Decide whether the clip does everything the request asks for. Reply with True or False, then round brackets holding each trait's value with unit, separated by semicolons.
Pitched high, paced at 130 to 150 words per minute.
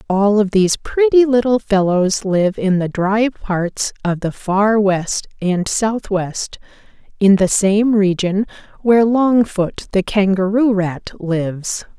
True (205 Hz; 135 wpm)